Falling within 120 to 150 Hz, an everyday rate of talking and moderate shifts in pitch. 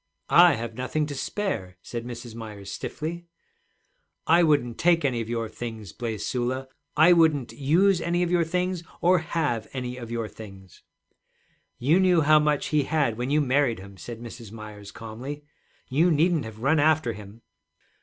No: low, 135 Hz; average, 170 wpm; wide, 5.8 semitones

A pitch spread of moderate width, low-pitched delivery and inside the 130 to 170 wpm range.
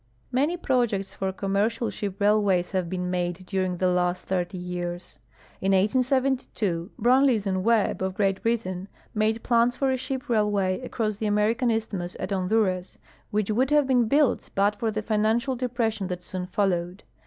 No: average, 4.0 semitones; high, 210 Hz; average, 165 wpm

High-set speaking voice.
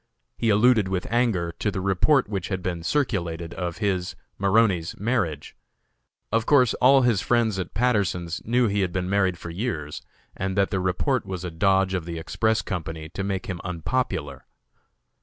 No: very low, 95 Hz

